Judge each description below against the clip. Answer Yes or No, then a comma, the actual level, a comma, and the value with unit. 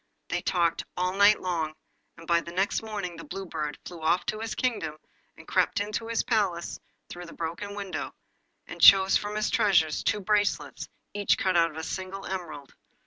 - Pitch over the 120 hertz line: Yes, medium, 185 Hz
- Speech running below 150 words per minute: No, average, 185 wpm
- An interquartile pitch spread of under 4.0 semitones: Yes, average, 3.5 semitones